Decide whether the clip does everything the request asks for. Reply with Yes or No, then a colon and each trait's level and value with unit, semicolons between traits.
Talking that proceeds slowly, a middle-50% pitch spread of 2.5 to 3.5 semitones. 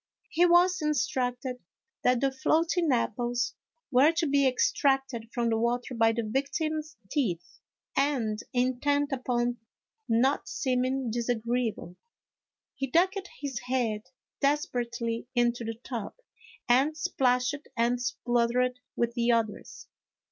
Yes: slow, 115 wpm; average, 3.1 semitones